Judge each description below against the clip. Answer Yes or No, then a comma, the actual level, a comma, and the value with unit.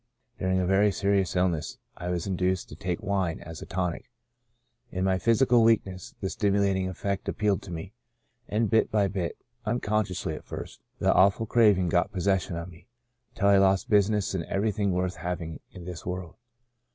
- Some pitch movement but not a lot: No, narrow, 2.1 semitones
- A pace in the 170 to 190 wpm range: Yes, average, 175 wpm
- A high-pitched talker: No, very low, 95 Hz